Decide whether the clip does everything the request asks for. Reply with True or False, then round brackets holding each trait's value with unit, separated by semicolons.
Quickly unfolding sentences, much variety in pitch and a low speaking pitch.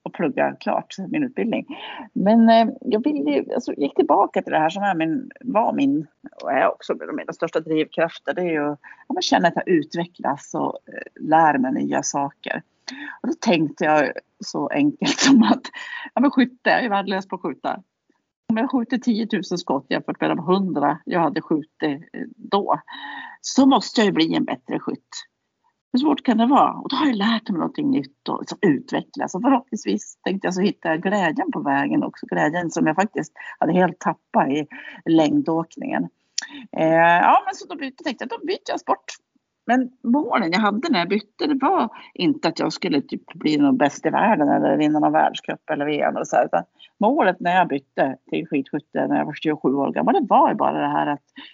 False (200 wpm; 9.0 semitones; 235 Hz)